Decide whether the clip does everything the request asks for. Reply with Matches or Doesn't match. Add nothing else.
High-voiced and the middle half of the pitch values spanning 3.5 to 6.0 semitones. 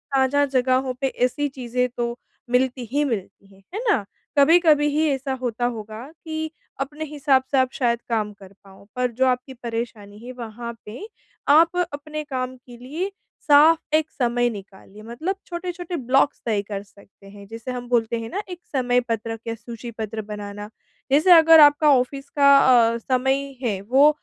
Matches